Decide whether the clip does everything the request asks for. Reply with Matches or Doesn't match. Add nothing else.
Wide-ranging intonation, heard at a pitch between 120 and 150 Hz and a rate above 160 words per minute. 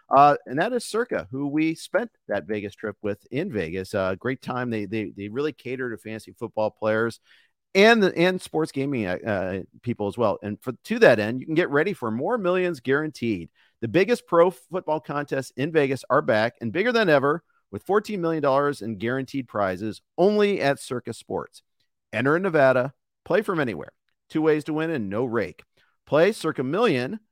Matches